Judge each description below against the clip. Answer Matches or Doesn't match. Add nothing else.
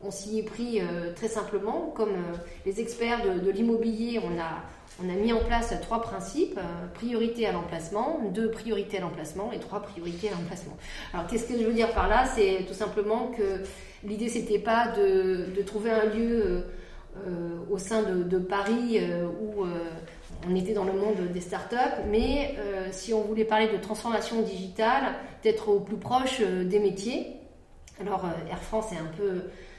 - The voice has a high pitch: Matches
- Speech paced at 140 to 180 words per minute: Doesn't match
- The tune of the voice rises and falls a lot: Doesn't match